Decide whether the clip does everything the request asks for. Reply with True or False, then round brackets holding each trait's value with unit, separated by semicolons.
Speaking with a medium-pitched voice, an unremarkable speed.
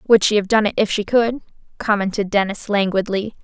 False (205 Hz; 190 wpm)